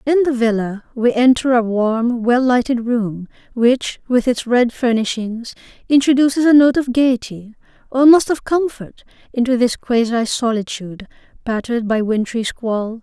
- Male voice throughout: No, female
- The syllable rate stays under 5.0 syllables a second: Yes, 4.8 syllables/s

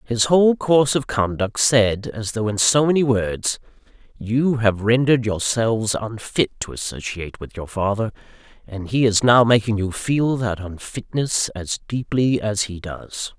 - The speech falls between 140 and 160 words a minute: Yes, average, 155 wpm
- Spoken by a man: Yes, male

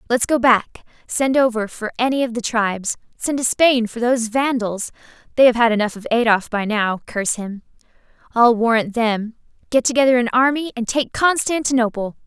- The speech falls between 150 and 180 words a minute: Yes, average, 165 wpm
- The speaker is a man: No, female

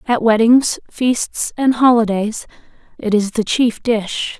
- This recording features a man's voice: No, female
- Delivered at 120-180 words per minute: Yes, slow, 135 wpm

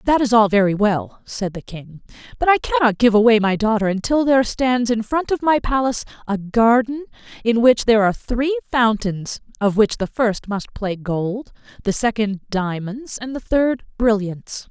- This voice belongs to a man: No, female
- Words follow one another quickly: No, average, 185 wpm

